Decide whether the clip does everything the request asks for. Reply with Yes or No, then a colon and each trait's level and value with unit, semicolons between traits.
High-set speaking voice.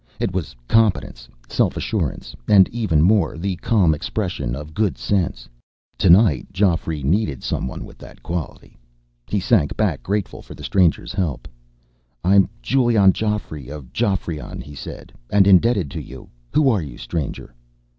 No: very low, 90 Hz